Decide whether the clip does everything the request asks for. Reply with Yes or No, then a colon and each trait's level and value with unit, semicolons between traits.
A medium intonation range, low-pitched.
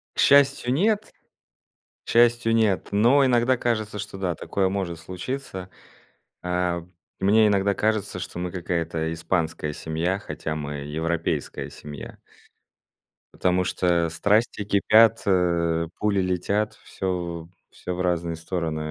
Yes: average, 4.2 semitones; very low, 90 Hz